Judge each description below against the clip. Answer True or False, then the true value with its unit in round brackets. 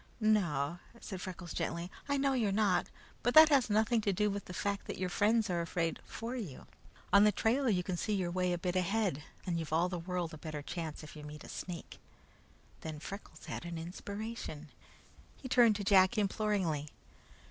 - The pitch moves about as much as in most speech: True (4.0 semitones)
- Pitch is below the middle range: False (185 Hz)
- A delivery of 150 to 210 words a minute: True (200 wpm)